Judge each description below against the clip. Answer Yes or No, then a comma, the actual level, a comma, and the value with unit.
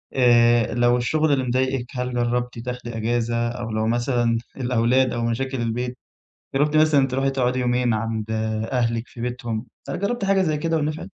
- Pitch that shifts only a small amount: Yes, narrow, 2.1 semitones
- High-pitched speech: No, low, 125 Hz